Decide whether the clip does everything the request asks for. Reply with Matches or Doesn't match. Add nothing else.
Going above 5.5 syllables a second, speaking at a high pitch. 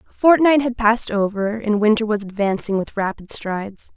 Doesn't match